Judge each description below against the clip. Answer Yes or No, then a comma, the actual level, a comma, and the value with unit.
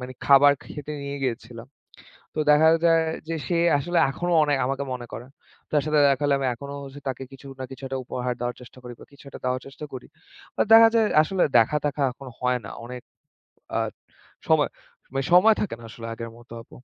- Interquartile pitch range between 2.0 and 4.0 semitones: Yes, average, 3.0 semitones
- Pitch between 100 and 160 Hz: Yes, low, 135 Hz